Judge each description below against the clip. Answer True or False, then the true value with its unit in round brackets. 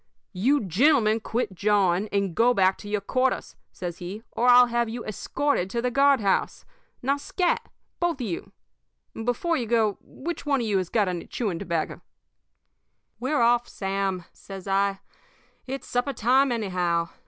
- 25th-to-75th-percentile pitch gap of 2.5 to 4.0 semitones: False (4.5 semitones)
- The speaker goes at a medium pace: True (165 wpm)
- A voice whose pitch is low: False (220 Hz)